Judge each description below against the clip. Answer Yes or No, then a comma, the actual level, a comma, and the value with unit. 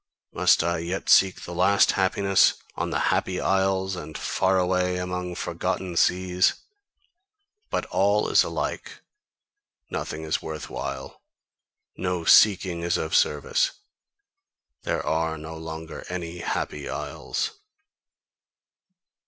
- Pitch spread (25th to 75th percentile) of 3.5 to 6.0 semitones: No, narrow, 2.5 semitones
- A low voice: Yes, very low, 90 Hz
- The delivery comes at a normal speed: No, slow, 115 wpm